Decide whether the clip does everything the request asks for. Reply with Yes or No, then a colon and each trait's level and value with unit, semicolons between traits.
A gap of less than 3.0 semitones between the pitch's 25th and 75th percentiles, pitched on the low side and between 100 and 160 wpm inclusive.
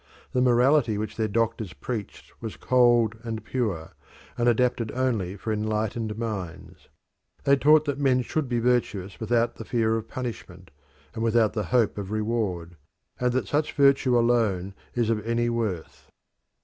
Yes: narrow, 2.6 semitones; low, 115 Hz; average, 155 wpm